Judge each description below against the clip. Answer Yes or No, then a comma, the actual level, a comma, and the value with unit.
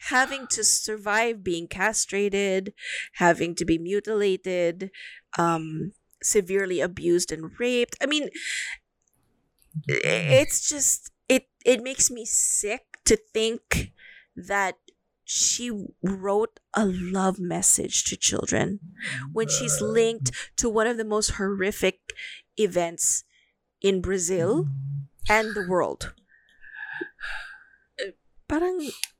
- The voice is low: No, high, 205 Hz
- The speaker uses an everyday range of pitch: Yes, average, 4.6 semitones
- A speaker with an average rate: No, slow, 105 wpm